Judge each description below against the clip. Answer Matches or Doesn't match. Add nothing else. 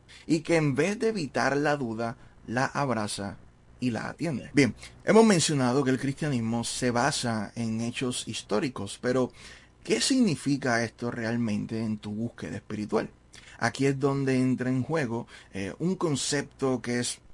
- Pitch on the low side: Matches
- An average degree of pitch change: Matches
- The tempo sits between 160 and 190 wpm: Doesn't match